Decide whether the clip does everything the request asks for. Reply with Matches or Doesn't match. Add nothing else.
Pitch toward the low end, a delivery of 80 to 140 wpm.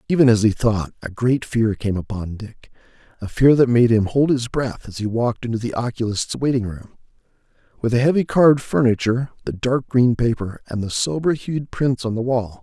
Doesn't match